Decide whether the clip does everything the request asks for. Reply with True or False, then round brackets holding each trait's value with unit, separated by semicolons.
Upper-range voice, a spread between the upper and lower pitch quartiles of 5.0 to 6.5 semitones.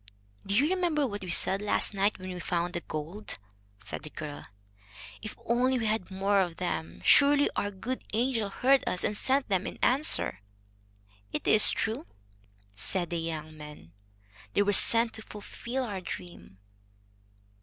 True (205 Hz; 5.5 semitones)